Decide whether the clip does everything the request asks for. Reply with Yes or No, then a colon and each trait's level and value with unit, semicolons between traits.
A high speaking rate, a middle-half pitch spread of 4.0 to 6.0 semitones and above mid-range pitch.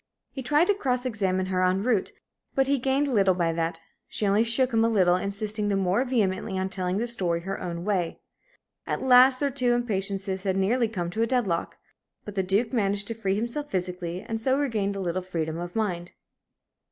Yes: fast, 210 wpm; average, 4.5 semitones; high, 200 Hz